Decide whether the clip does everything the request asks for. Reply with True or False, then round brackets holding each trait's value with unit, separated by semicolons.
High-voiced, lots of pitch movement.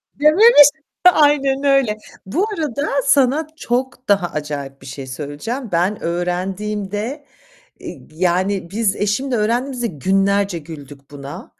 True (205 Hz; 7.8 semitones)